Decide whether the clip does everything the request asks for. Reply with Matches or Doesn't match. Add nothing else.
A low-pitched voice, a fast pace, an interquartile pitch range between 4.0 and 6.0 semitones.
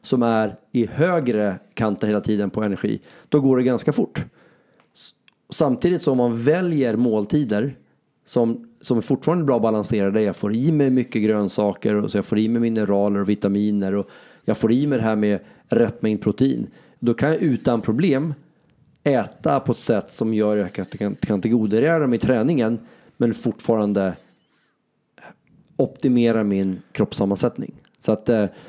Doesn't match